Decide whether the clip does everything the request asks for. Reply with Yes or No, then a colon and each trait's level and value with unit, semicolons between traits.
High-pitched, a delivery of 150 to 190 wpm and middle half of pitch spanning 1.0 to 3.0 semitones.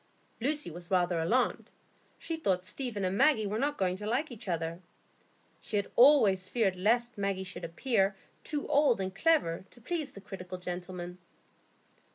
No: high, 200 Hz; average, 165 wpm; average, 5.3 semitones